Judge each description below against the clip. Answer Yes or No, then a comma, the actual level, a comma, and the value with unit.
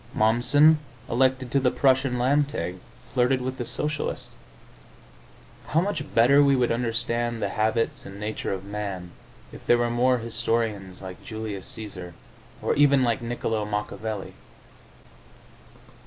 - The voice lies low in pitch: Yes, low, 120 Hz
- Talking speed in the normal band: No, slow, 130 wpm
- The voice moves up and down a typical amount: Yes, average, 3.5 semitones